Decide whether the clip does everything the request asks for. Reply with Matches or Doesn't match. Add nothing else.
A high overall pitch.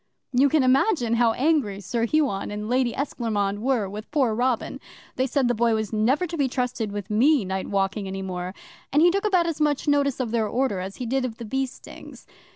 Matches